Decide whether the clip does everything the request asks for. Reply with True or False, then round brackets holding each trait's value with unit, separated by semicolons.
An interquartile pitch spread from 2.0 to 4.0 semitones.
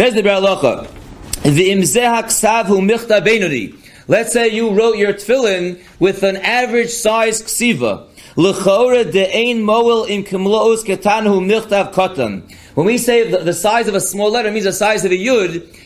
True (2.9 semitones)